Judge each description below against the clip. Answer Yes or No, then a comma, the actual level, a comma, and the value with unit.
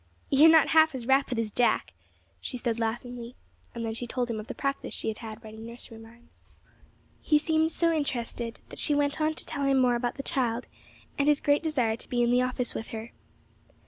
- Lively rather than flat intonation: No, average, 3.8 semitones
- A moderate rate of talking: No, fast, 220 wpm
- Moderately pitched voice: No, high, 245 Hz